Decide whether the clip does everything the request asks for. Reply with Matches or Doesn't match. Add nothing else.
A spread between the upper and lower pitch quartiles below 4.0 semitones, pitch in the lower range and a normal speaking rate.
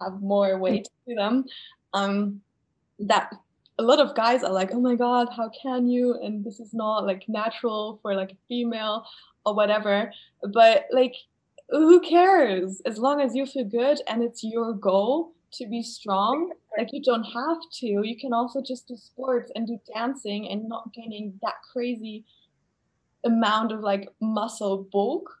Doesn't match